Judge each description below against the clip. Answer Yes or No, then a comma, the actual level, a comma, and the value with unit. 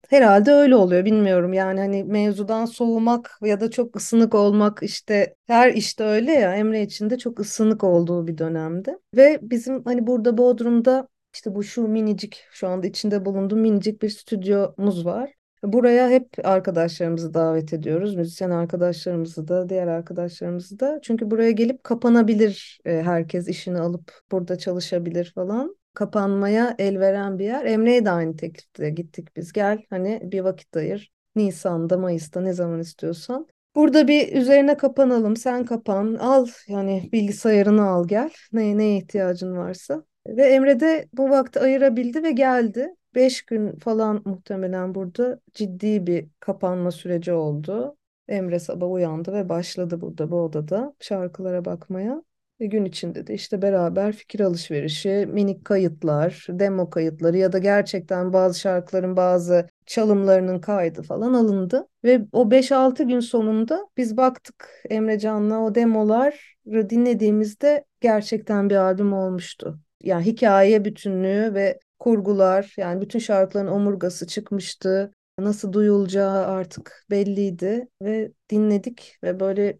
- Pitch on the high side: Yes, high, 205 Hz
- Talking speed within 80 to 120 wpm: No, fast, 140 wpm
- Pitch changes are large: No, average, 4.0 semitones